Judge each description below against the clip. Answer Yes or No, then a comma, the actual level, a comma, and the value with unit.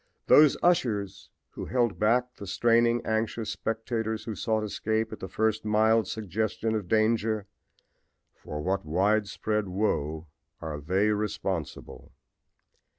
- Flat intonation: Yes, narrow, 2.2 semitones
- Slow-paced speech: Yes, slow, 120 wpm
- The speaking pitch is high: No, low, 110 Hz